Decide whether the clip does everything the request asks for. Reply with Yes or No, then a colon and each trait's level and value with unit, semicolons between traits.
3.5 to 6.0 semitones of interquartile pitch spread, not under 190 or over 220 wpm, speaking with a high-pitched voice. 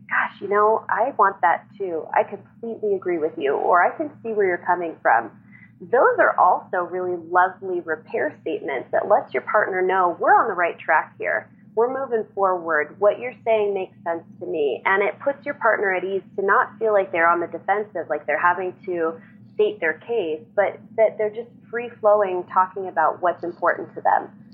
Yes: average, 3.9 semitones; average, 200 wpm; high, 195 Hz